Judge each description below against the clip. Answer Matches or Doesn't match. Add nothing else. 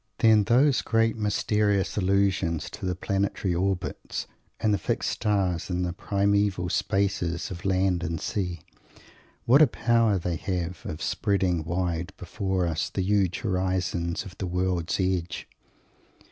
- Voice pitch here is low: Matches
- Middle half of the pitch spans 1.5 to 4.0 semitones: Matches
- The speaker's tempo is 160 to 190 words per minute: Doesn't match